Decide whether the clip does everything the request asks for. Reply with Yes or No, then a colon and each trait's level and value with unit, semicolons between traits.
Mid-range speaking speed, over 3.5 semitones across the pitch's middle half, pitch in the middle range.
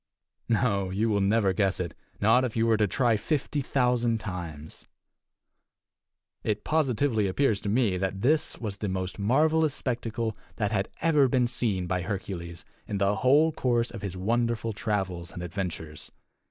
No: average, 160 wpm; average, 4.2 semitones; low, 110 Hz